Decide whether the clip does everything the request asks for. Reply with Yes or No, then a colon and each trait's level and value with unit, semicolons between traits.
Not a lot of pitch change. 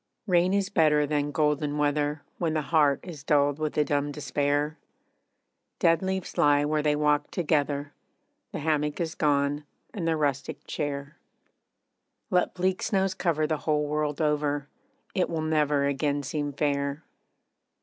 Yes: narrow, 1.7 semitones